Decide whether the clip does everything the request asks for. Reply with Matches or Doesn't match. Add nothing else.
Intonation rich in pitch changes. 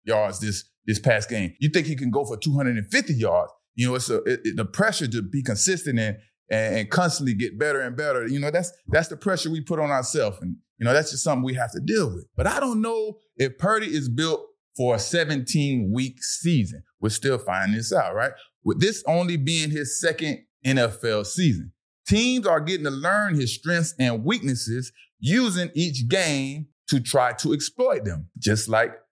Matches